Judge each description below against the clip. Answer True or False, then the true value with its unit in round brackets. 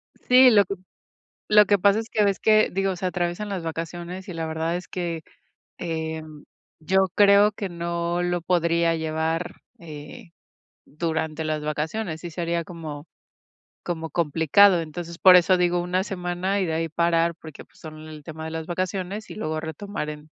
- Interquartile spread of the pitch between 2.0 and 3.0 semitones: True (2.7 semitones)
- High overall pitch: False (170 Hz)